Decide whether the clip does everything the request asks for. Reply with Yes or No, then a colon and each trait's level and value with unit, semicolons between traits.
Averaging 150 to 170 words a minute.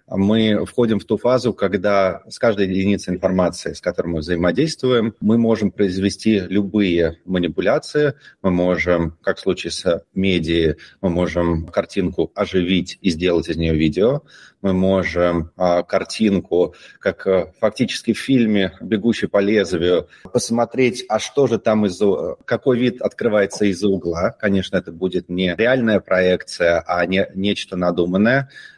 No: average, 140 wpm